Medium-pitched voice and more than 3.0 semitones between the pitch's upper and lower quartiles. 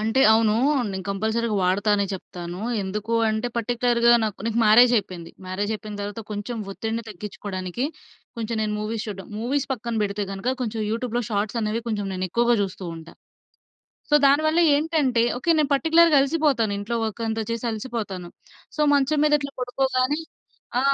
No: high, 225 Hz; average, 3.4 semitones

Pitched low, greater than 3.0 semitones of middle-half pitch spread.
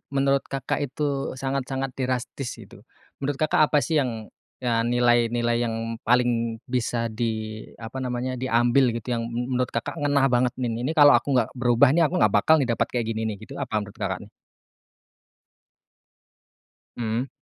No: low, 125 Hz; average, 2.7 semitones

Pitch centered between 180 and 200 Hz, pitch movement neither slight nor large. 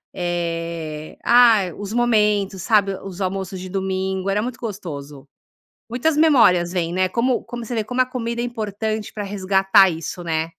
Yes: high, 195 Hz; average, 4.2 semitones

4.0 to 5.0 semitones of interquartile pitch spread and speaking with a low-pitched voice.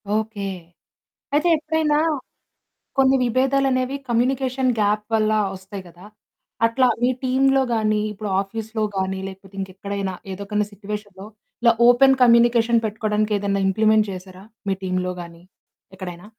No: average, 4.3 semitones; high, 215 Hz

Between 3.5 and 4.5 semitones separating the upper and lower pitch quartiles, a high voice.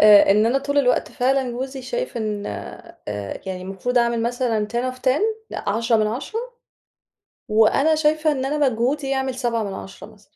Yes: average, 4.0 semitones; high, 245 Hz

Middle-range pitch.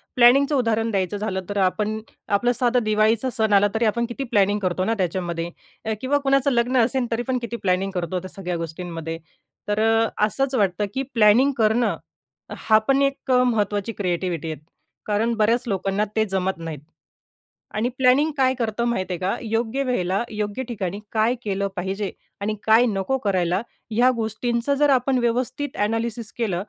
No: high, 220 Hz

